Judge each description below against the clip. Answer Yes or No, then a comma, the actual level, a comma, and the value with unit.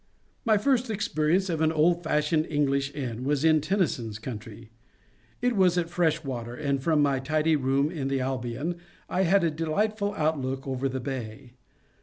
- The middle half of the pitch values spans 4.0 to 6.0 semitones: Yes, average, 4.3 semitones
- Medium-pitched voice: Yes, medium, 150 Hz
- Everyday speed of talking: Yes, average, 165 wpm